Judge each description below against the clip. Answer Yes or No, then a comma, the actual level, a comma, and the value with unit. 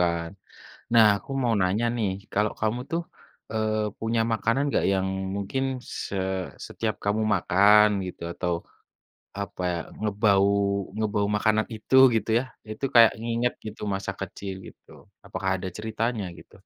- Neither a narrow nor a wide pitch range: No, narrow, 2.2 semitones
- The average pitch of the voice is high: No, low, 105 Hz